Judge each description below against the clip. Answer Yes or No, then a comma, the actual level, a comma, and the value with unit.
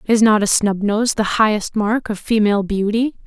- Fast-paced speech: No, average, 185 wpm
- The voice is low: No, high, 215 Hz